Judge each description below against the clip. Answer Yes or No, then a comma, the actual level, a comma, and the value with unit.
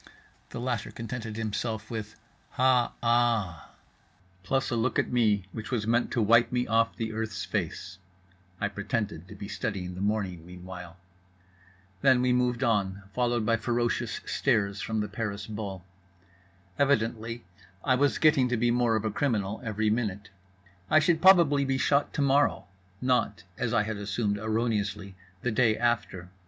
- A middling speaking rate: Yes, average, 155 wpm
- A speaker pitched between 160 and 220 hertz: No, low, 115 Hz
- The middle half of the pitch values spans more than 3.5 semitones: No, average, 3.1 semitones